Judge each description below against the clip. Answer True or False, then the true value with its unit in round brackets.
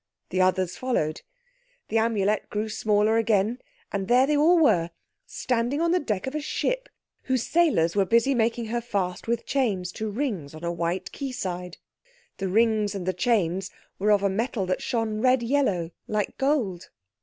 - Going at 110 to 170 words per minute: False (180 wpm)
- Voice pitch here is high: True (215 Hz)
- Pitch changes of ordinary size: True (5.0 semitones)